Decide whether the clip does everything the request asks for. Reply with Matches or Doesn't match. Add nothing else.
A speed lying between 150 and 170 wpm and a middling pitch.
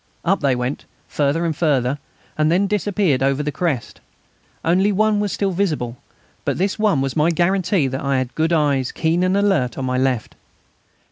Doesn't match